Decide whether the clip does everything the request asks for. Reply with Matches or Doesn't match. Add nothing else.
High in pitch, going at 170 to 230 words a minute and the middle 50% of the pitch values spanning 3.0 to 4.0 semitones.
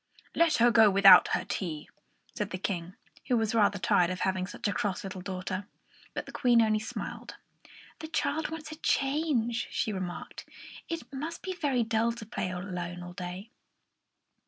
Doesn't match